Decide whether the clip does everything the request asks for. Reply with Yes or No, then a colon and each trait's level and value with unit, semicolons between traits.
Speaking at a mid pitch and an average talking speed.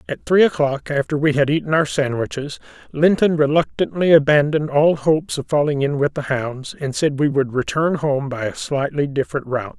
Yes: medium, 145 Hz; average, 190 wpm